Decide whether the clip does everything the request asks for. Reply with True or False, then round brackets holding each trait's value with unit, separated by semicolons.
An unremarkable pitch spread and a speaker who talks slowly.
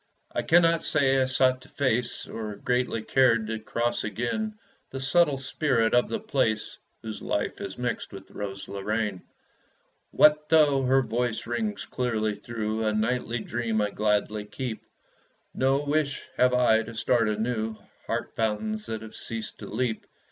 False (3.5 semitones; 155 wpm)